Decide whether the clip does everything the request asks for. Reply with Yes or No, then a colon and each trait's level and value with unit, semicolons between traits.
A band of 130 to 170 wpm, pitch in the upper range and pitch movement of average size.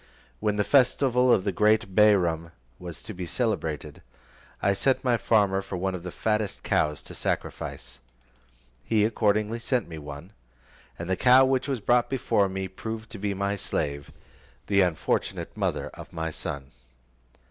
No: average, 160 wpm; low, 100 Hz; average, 4.4 semitones